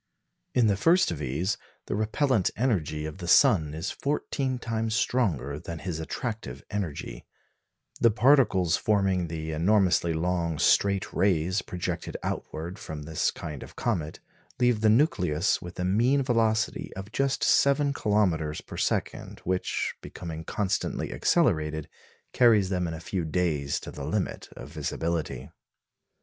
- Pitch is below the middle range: Yes, very low, 95 Hz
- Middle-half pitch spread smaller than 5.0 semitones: No, wide, 5.6 semitones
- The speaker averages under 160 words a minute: Yes, average, 140 wpm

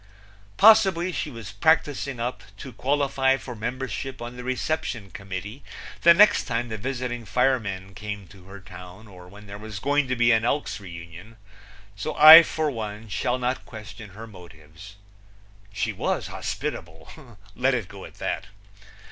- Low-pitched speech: Yes, low, 115 Hz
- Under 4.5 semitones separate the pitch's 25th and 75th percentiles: No, average, 5.0 semitones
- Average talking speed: Yes, average, 155 wpm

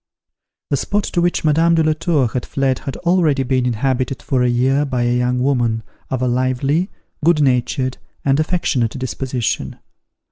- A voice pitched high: No, low, 135 Hz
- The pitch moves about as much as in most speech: Yes, average, 3.5 semitones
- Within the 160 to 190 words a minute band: Yes, average, 170 wpm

